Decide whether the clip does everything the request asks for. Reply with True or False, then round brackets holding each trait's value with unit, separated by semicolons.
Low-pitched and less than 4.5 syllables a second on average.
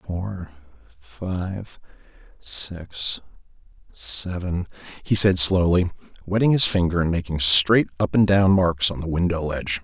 True (90 Hz; 4.0 syllables/s)